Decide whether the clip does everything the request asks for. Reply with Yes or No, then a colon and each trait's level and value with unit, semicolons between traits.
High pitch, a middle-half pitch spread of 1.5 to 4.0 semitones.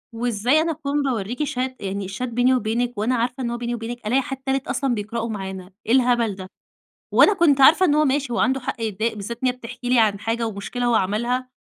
Yes: high, 240 Hz; average, 2.9 semitones